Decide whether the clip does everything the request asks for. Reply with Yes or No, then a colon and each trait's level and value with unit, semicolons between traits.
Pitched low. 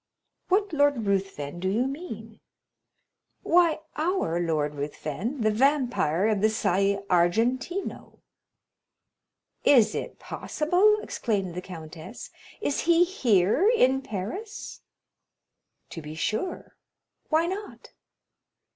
No: high, 225 Hz